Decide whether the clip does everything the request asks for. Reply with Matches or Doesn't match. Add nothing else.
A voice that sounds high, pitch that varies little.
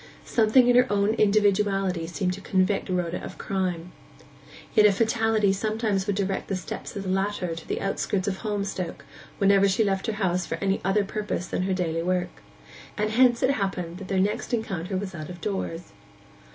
Matches